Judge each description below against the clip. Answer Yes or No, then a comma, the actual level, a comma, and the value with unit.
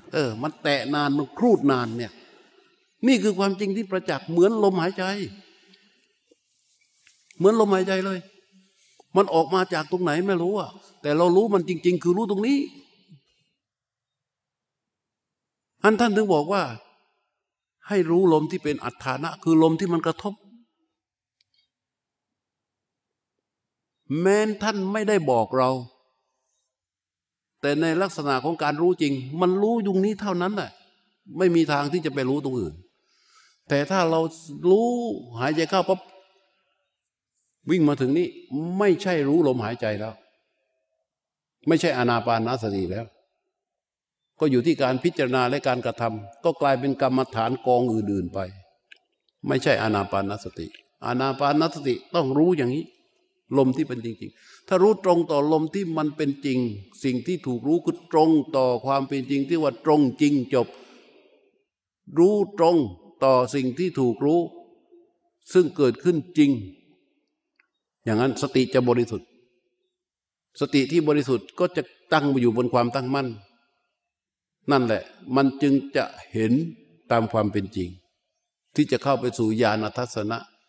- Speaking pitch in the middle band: Yes, medium, 150 Hz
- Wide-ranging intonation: Yes, wide, 6.8 semitones